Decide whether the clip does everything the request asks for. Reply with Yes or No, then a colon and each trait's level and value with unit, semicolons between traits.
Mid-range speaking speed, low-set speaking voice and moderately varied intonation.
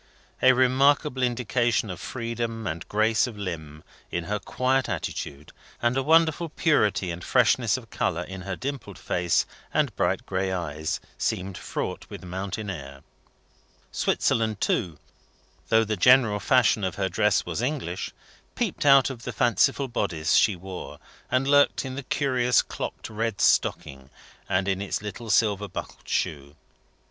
No: average, 150 wpm; low, 105 Hz; wide, 5.7 semitones